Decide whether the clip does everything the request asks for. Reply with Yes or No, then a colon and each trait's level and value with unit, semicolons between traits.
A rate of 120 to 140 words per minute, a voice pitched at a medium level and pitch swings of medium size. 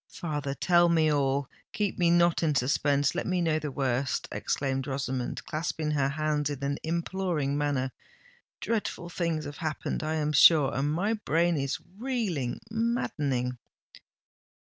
Yes: slow, 135 wpm; medium, 150 Hz; average, 3.7 semitones